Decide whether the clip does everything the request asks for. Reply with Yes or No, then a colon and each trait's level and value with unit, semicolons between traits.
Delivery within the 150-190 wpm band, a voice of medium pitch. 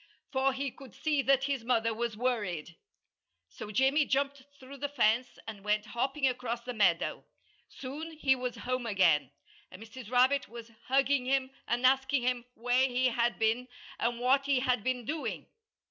No: average, 170 wpm; very high, 250 Hz